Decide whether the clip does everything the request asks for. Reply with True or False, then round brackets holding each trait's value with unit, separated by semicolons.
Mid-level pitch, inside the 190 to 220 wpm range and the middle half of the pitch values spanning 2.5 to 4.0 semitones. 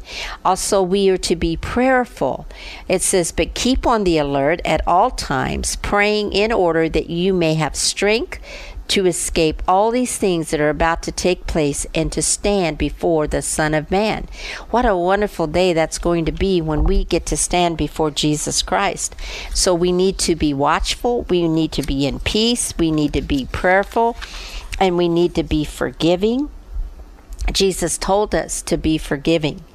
False (175 Hz; 175 wpm; 3.7 semitones)